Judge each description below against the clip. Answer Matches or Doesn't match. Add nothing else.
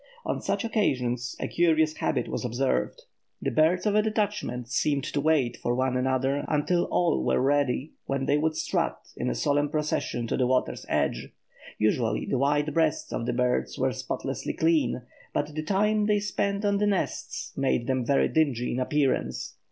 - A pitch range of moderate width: Matches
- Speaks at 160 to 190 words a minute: Matches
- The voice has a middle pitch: Matches